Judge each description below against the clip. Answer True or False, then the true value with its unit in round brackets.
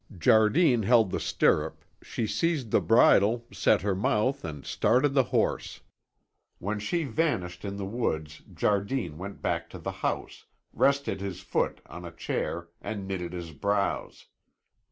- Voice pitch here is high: False (100 Hz)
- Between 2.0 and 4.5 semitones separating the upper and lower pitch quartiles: False (5.2 semitones)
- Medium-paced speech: True (150 wpm)